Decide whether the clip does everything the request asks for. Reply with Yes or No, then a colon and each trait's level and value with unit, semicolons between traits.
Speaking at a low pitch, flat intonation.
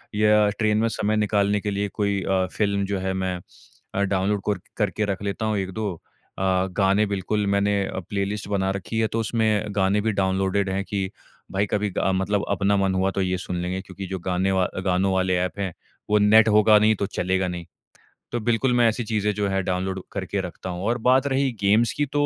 Yes: low, 100 Hz; narrow, 2.0 semitones